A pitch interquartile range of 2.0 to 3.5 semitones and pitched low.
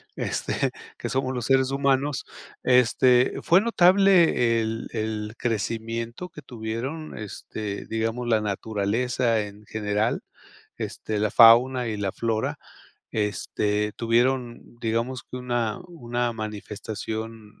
Yes: average, 2.8 semitones; low, 115 Hz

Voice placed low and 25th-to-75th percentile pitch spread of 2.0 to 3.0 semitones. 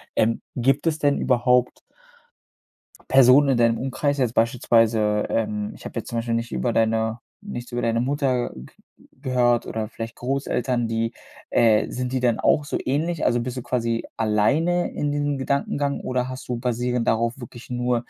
Yes: low, 120 Hz; narrow, 2.6 semitones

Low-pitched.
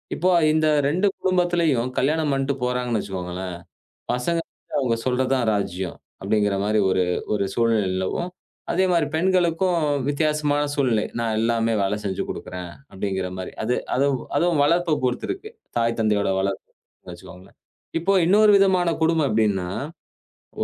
Yes: low, 125 Hz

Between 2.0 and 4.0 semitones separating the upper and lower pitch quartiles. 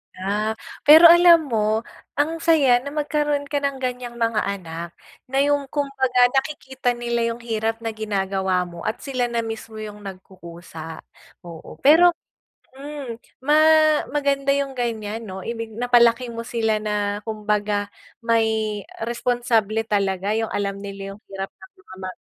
No: average, 4.5 semitones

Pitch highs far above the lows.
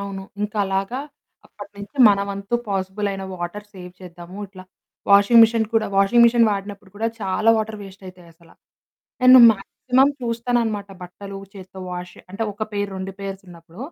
No: narrow, 2.6 semitones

